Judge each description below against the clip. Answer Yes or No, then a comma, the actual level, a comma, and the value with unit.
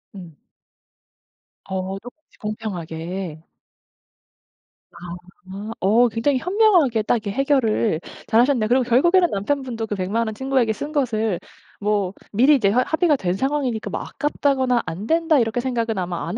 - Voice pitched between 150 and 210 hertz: No, high, 230 Hz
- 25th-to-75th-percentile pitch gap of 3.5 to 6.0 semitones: Yes, average, 5.1 semitones